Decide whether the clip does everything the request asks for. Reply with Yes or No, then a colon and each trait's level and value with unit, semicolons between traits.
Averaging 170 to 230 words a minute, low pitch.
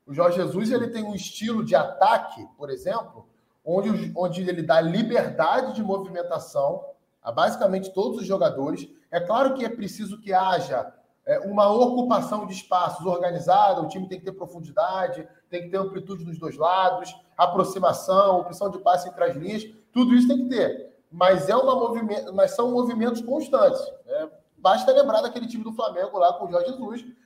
No: average, 180 wpm; high, 200 Hz